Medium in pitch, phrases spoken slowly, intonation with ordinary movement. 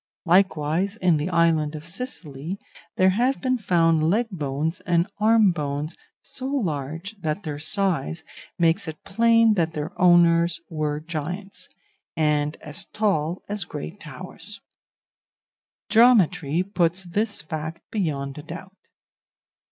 Yes: medium, 170 Hz; slow, 125 wpm; average, 4.3 semitones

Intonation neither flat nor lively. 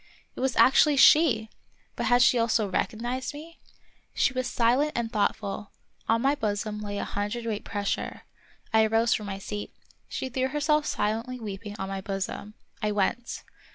Yes: average, 3.7 semitones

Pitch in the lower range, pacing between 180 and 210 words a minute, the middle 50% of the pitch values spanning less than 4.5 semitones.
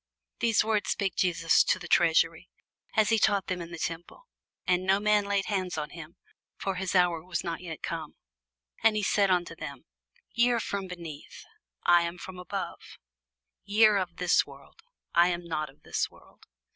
No: medium, 180 Hz; average, 185 wpm; average, 3.0 semitones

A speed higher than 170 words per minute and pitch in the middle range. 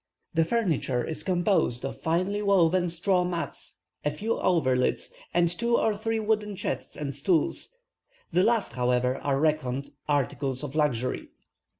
No: average, 140 wpm; medium, 165 Hz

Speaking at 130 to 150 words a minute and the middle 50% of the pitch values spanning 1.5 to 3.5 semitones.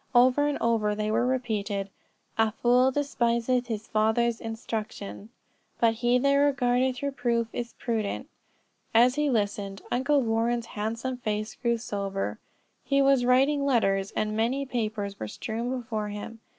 Yes: average, 140 wpm; average, 2.9 semitones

